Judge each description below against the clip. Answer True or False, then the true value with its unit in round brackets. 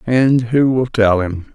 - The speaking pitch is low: True (115 Hz)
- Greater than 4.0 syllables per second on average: False (3.5 syllables/s)